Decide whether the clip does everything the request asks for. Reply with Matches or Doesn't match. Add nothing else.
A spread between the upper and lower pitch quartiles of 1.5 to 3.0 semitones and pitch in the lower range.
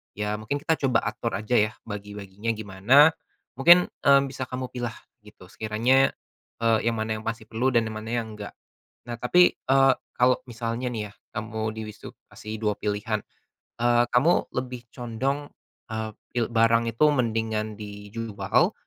Matches